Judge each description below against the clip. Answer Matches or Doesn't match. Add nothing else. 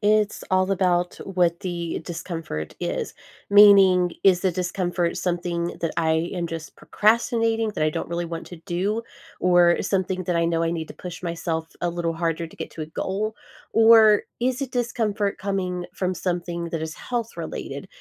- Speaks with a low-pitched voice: Doesn't match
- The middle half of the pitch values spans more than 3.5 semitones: Doesn't match